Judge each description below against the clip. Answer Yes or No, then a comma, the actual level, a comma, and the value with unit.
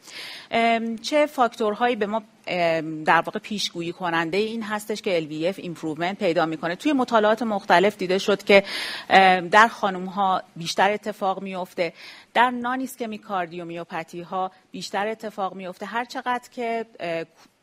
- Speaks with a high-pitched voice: Yes, high, 200 Hz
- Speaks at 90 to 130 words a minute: Yes, average, 125 wpm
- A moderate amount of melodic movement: Yes, average, 4.2 semitones